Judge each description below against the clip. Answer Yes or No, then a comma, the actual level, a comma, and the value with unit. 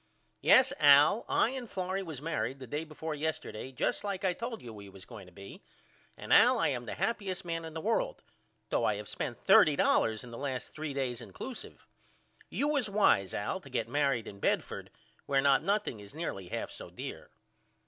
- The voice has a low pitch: No, medium, 150 Hz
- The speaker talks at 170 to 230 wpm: Yes, average, 200 wpm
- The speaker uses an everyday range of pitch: No, wide, 8.1 semitones